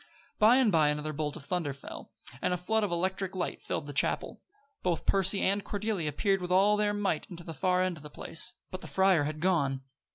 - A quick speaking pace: Yes, fast, 225 wpm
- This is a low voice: No, medium, 180 Hz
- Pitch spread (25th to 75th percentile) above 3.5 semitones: Yes, average, 4.1 semitones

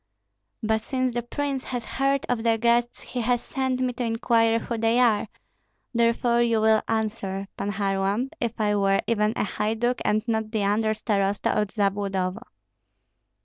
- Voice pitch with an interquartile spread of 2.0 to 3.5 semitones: Yes, narrow, 2.4 semitones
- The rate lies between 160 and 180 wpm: Yes, average, 165 wpm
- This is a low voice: No, high, 225 Hz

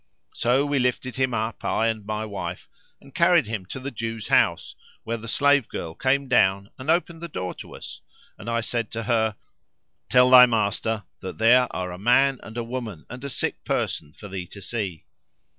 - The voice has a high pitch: No, low, 115 Hz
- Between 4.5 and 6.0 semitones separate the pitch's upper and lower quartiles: No, average, 3.5 semitones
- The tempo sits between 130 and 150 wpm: No, average, 200 wpm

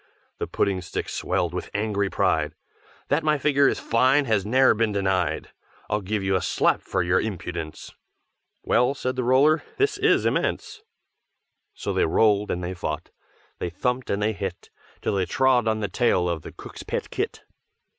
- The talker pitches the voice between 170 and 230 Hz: No, low, 105 Hz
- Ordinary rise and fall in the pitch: No, wide, 5.8 semitones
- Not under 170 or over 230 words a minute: Yes, average, 175 wpm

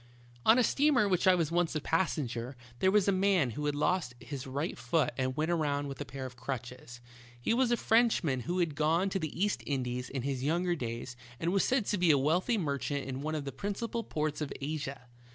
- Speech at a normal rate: No, fast, 230 wpm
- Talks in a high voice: No, medium, 155 Hz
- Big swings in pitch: Yes, wide, 5.7 semitones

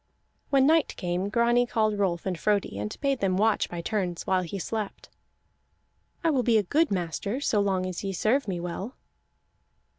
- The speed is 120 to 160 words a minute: No, average, 180 wpm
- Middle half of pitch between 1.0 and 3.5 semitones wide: No, average, 4.5 semitones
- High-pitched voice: Yes, high, 200 Hz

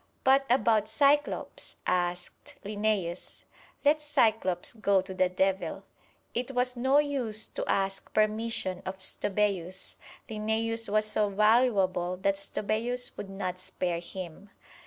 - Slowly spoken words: Yes, slow, 120 wpm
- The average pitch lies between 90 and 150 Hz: No, high, 210 Hz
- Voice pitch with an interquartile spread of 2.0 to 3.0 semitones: No, average, 3.7 semitones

